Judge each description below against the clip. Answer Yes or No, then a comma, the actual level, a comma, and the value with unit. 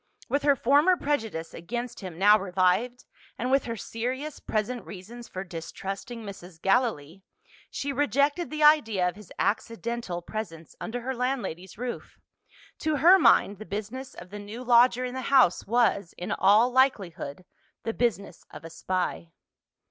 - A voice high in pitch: Yes, high, 225 Hz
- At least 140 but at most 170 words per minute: Yes, average, 155 wpm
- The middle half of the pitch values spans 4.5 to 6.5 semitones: Yes, average, 5.2 semitones